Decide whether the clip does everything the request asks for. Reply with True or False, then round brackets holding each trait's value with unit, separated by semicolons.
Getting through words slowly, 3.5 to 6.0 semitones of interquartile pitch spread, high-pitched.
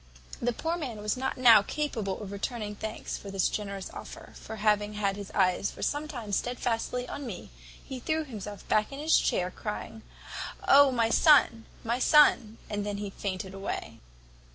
False (175 wpm; 4.0 semitones; 220 Hz)